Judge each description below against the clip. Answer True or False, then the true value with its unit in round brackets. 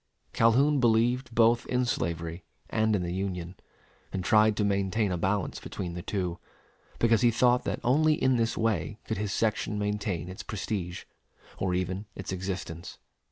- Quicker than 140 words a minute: True (160 wpm)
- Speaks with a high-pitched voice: False (105 Hz)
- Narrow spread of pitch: False (3.9 semitones)